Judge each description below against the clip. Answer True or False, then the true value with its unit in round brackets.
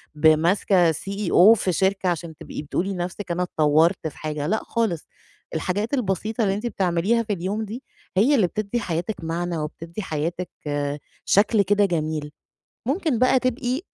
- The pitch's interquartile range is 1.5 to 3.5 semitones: False (4.5 semitones)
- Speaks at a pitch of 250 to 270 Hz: False (190 Hz)